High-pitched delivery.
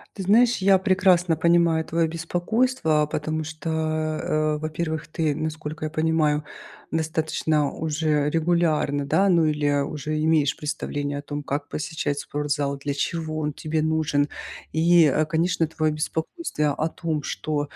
No: medium, 155 Hz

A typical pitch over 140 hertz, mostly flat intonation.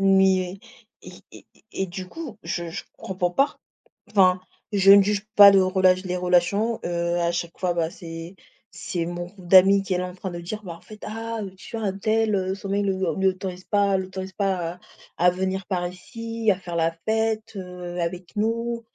Yes: high, 190 Hz; narrow, 2.3 semitones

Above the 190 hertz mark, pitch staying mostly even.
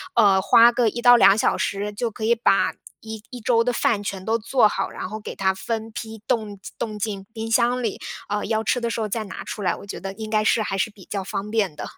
Yes: high, 215 Hz; narrow, 2.3 semitones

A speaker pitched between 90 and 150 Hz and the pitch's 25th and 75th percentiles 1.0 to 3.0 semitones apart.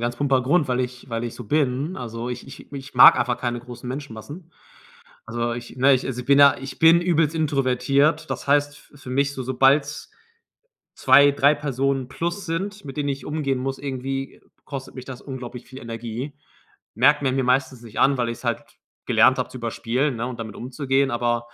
Yes: low, 135 Hz; narrow, 2.5 semitones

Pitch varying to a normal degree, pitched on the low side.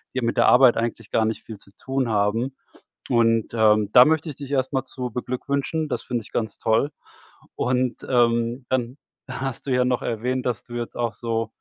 No: narrow, 2.2 semitones; low, 120 Hz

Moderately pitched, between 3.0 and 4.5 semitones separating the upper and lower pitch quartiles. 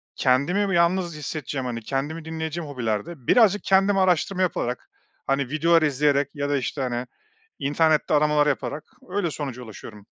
Yes: medium, 150 Hz; average, 4.1 semitones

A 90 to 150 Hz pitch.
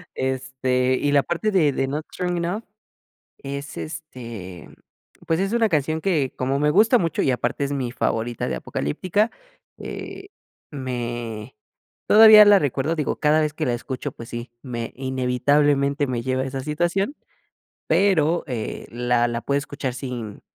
Yes: medium, 140 Hz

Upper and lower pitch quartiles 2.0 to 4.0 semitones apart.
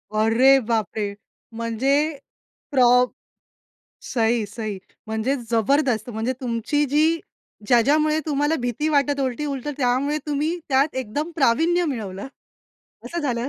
No: average, 4.5 semitones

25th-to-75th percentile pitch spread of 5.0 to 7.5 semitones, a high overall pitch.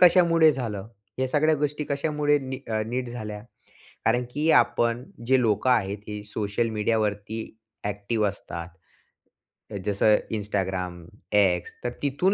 No: average, 5.3 semitones; low, 115 Hz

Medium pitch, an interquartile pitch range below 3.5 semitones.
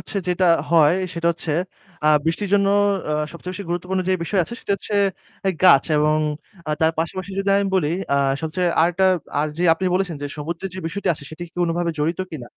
Yes: medium, 170 Hz; average, 2.9 semitones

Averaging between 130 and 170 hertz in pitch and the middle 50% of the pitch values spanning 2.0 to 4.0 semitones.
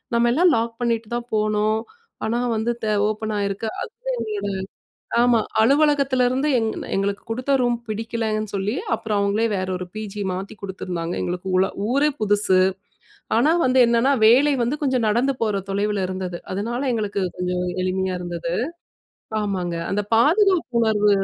No: high, 215 Hz; average, 3.5 semitones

